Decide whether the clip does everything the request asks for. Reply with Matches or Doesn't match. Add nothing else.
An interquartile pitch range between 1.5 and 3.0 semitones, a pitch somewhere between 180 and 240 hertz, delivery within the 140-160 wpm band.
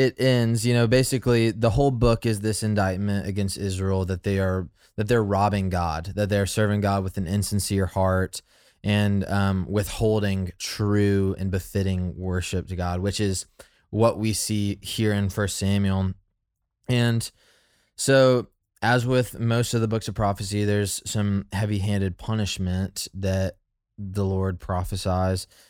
Doesn't match